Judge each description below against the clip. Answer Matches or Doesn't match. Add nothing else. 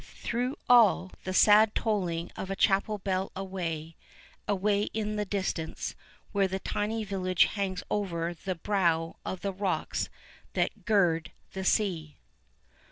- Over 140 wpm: Doesn't match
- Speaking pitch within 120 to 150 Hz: Doesn't match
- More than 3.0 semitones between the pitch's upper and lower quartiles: Doesn't match